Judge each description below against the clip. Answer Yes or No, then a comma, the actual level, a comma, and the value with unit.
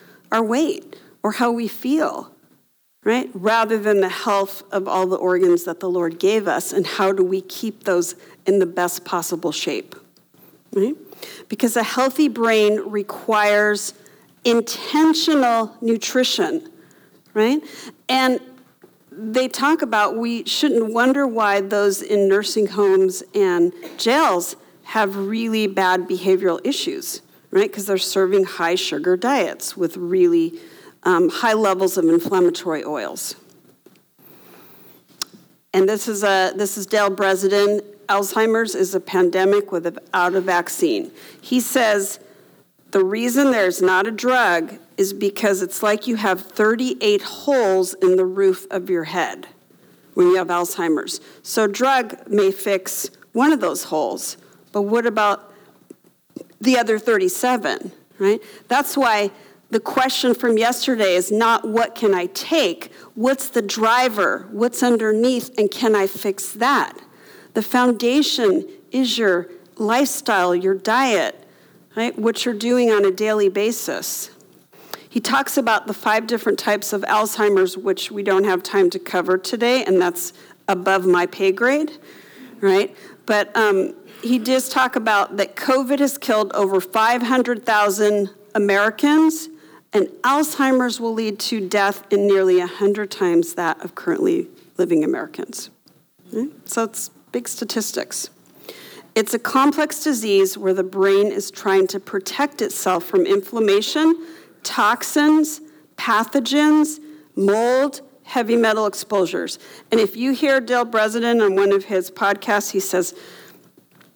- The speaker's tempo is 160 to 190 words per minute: No, slow, 135 wpm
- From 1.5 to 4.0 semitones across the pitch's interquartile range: No, average, 4.8 semitones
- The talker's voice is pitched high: Yes, high, 215 Hz